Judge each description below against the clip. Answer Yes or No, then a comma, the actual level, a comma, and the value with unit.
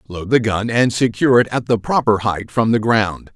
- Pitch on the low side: Yes, low, 110 Hz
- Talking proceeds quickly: Yes, fast, 230 wpm